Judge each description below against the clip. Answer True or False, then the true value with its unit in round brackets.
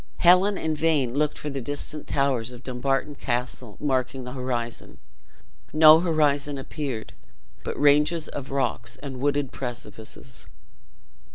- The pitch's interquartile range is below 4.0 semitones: True (3.0 semitones)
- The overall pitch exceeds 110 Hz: True (140 Hz)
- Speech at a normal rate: False (125 wpm)